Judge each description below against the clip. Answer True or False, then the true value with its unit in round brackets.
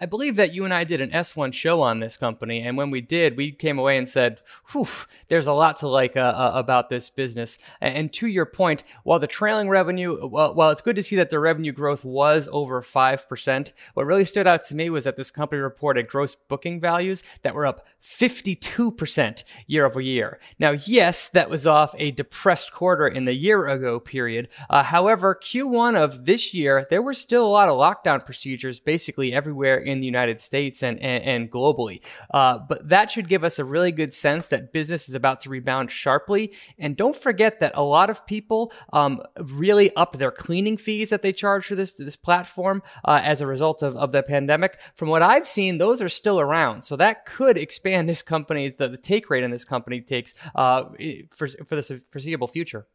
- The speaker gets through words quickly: True (215 wpm)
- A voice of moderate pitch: True (150 Hz)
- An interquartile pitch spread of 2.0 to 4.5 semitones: False (5.4 semitones)